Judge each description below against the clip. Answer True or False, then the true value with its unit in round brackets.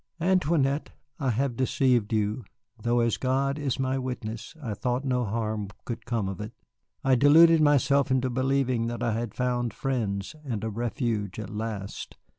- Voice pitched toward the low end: True (125 Hz)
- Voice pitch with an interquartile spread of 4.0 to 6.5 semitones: False (3.3 semitones)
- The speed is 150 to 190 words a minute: True (165 wpm)